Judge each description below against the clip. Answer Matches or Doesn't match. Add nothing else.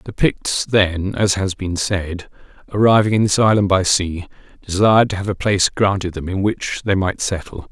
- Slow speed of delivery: Doesn't match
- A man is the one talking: Matches